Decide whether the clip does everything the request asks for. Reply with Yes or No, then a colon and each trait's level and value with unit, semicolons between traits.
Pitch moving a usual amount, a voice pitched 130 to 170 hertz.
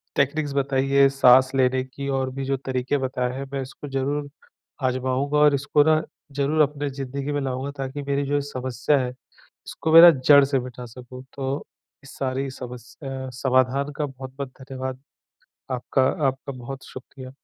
No: narrow, 1.5 semitones; low, 135 Hz